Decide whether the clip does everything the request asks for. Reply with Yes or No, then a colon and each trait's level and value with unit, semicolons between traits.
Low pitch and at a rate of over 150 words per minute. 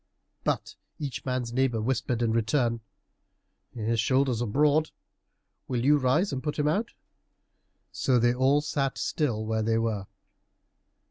No: low, 125 Hz; average, 140 wpm